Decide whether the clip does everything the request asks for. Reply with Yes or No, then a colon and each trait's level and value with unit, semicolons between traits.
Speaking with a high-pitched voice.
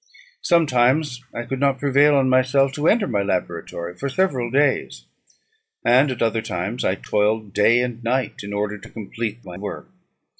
No: low, 120 Hz